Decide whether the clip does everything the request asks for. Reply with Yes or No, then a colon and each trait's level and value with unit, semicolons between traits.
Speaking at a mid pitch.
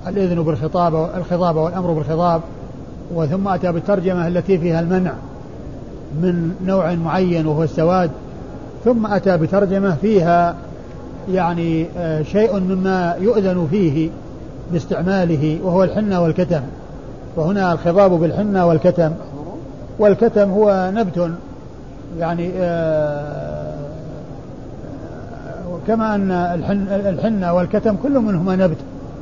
Yes: medium, 175 Hz